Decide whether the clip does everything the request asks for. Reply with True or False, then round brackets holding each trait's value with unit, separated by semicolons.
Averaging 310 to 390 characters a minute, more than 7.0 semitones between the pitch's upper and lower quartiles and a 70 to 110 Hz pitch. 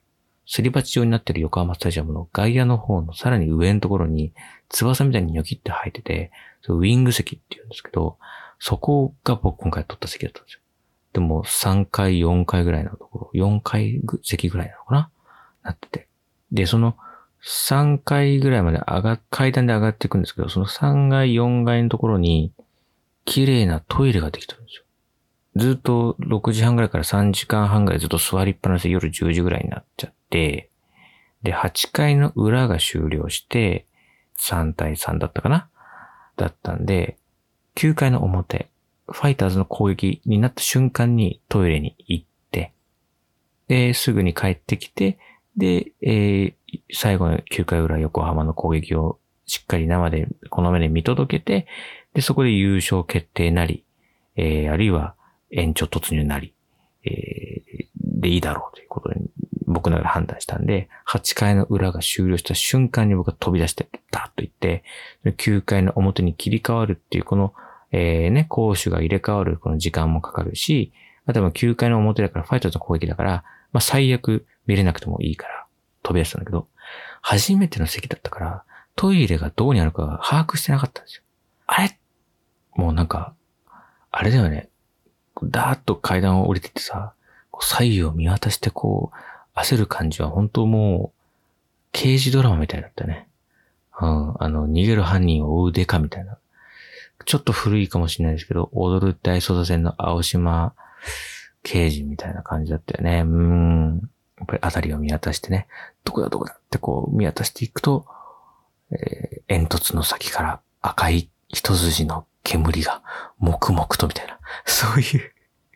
False (320 characters per minute; 5.6 semitones; 95 Hz)